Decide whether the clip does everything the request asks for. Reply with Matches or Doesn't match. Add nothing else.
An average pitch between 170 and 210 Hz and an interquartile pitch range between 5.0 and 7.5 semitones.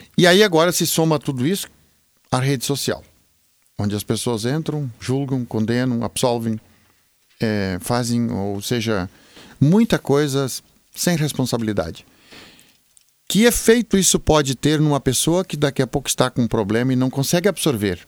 Doesn't match